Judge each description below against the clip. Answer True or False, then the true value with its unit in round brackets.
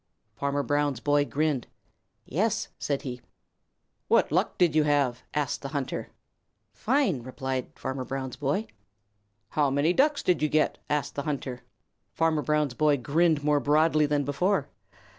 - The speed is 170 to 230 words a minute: False (145 wpm)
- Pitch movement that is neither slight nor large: False (2.1 semitones)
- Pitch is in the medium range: True (145 Hz)